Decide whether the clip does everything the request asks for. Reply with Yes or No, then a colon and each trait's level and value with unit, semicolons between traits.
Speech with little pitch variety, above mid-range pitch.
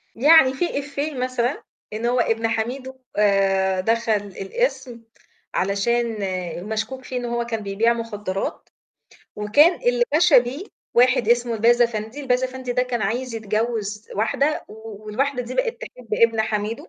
No: average, 3.1 semitones; high, 235 Hz